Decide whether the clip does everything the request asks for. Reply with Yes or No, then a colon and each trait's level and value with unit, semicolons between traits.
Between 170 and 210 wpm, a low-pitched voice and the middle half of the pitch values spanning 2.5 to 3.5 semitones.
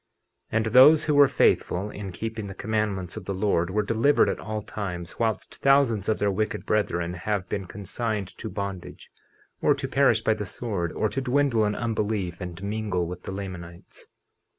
Yes: average, 185 wpm; low, 105 Hz; average, 3.2 semitones